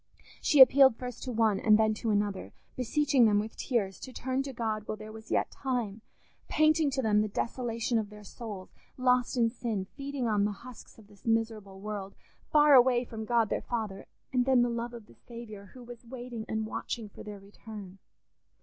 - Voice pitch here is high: Yes, high, 230 Hz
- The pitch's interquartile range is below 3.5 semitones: Yes, average, 2.9 semitones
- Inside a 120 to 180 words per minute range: No, average, 200 wpm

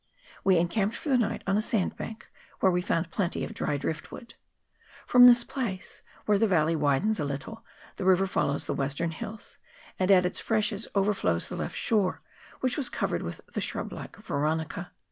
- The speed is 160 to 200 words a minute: Yes, average, 185 wpm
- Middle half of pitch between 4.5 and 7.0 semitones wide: Yes, average, 5.2 semitones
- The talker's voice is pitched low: No, high, 190 Hz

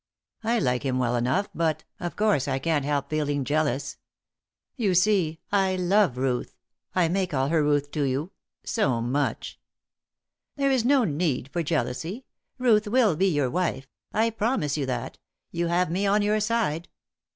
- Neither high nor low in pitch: Yes, medium, 165 Hz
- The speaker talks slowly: No, average, 165 wpm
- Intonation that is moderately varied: No, wide, 6.3 semitones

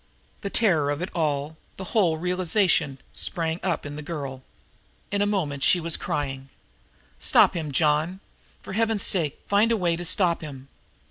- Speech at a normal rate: Yes, average, 170 wpm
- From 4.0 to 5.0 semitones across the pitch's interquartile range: Yes, average, 4.5 semitones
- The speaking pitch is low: No, medium, 165 Hz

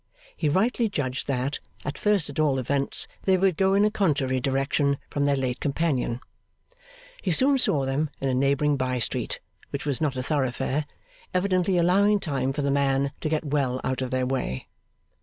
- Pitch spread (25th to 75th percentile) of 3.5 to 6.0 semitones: Yes, average, 4.4 semitones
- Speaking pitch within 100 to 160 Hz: Yes, medium, 140 Hz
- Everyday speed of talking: Yes, average, 185 wpm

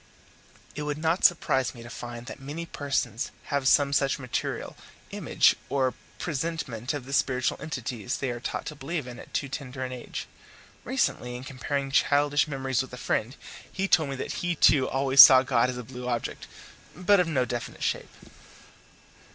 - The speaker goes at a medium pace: Yes, average, 180 wpm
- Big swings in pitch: No, average, 2.7 semitones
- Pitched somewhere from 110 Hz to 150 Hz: Yes, low, 135 Hz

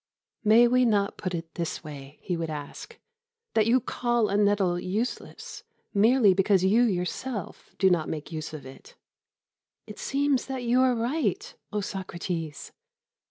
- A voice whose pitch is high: Yes, high, 205 Hz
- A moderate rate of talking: Yes, average, 160 wpm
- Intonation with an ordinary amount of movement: No, wide, 5.7 semitones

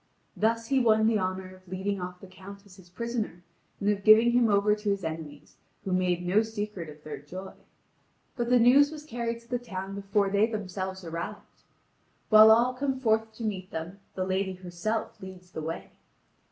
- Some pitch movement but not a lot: Yes, average, 3.3 semitones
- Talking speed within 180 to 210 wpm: Yes, average, 195 wpm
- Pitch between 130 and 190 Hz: No, high, 200 Hz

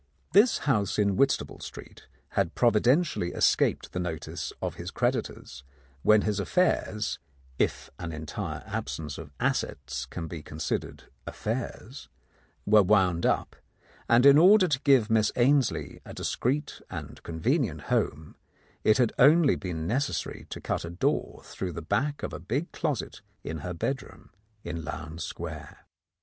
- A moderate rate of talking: Yes, average, 150 wpm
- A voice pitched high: No, low, 105 Hz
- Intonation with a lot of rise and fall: Yes, wide, 8.5 semitones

